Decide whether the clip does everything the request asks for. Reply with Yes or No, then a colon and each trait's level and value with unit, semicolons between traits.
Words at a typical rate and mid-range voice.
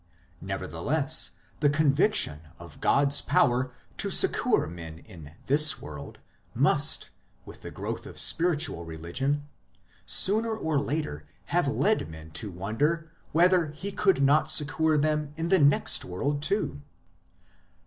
No: slow, 130 wpm; medium, 145 Hz